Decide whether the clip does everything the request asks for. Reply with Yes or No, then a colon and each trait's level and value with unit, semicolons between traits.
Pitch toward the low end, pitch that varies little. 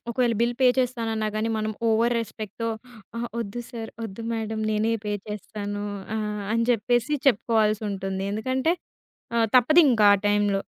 No: high, 220 Hz; narrow, 2.1 semitones